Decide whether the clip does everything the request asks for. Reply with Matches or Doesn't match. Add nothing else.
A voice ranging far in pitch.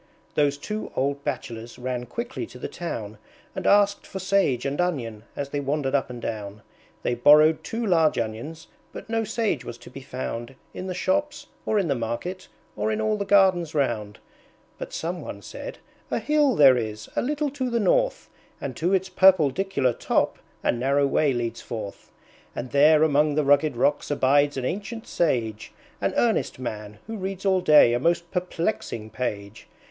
Matches